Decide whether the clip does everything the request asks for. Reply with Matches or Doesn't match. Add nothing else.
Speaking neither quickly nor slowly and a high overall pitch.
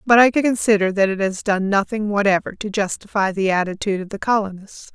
Matches